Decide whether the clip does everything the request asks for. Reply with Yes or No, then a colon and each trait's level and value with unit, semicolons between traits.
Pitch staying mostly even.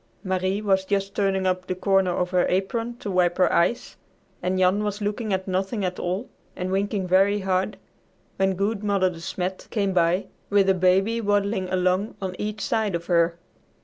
Yes: narrow, 1.9 semitones